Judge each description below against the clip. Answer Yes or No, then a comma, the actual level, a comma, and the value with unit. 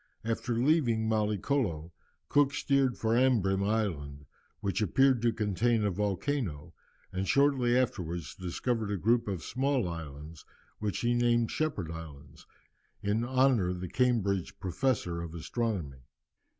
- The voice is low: Yes, low, 105 Hz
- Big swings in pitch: Yes, wide, 5.7 semitones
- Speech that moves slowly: Yes, slow, 130 wpm